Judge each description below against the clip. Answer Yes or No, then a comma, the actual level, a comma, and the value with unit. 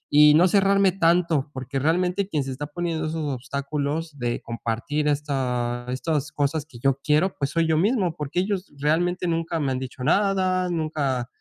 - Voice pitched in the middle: Yes, medium, 150 Hz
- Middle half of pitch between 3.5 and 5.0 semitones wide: Yes, average, 4.1 semitones